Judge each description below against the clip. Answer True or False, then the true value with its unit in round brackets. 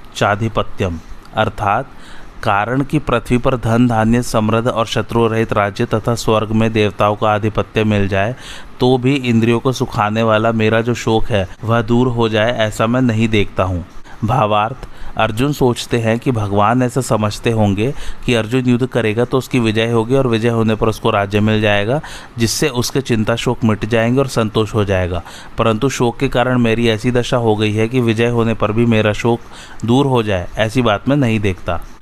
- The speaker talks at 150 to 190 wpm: True (185 wpm)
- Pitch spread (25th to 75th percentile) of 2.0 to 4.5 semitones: True (2.4 semitones)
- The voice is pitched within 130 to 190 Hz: False (115 Hz)